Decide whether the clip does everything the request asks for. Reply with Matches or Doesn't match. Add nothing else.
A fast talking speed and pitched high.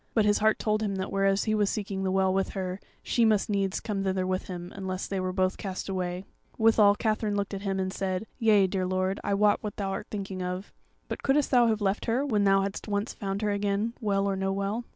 Matches